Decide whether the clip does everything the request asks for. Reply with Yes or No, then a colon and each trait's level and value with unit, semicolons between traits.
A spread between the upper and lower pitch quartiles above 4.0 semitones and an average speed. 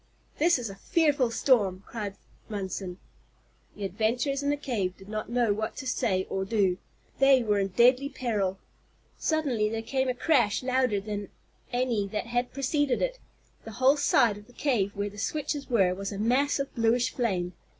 Yes: average, 4.6 semitones; average, 180 wpm